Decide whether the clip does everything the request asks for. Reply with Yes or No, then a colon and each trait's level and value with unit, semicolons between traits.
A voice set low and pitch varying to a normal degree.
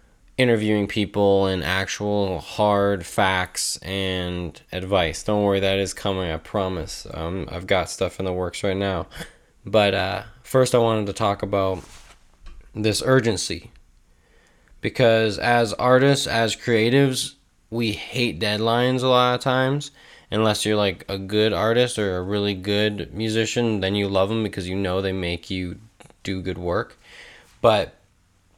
Yes: low, 100 Hz; average, 3.1 semitones